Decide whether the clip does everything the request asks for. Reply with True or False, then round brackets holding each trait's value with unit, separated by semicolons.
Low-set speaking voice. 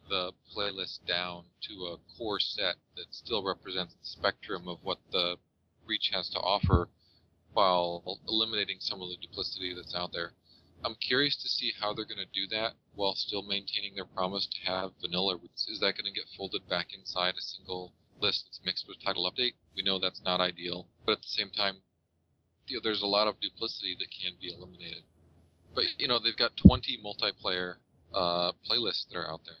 True (90 Hz)